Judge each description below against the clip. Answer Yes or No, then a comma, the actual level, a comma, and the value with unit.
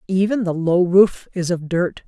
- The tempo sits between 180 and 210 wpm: Yes, average, 200 wpm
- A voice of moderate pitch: Yes, medium, 180 Hz